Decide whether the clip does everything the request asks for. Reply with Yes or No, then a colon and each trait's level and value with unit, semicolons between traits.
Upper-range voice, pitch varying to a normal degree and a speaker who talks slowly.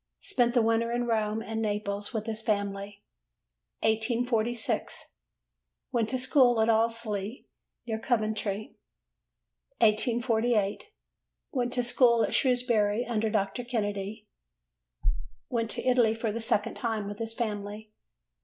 No: high, 225 Hz; narrow, 2.2 semitones; slow, 120 wpm